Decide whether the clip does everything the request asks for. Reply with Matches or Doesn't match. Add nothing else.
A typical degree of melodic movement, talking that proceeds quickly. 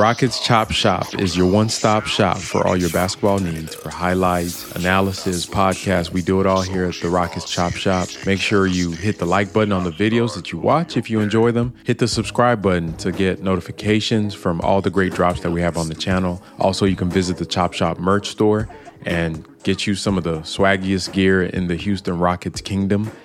Matches